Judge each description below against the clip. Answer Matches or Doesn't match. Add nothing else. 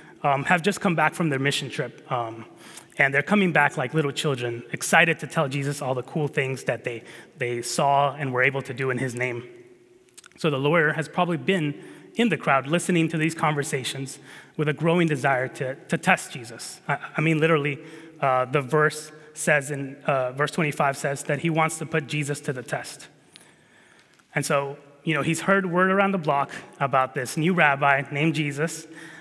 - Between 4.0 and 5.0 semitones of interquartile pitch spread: Doesn't match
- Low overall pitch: Doesn't match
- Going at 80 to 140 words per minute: Doesn't match